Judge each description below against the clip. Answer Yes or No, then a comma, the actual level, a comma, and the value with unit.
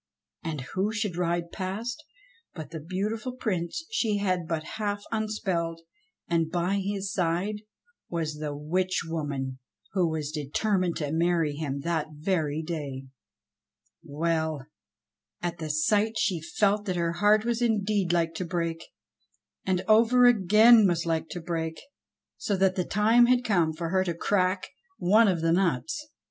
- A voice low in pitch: No, medium, 175 Hz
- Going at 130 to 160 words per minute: Yes, average, 150 wpm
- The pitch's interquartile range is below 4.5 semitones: Yes, average, 4.1 semitones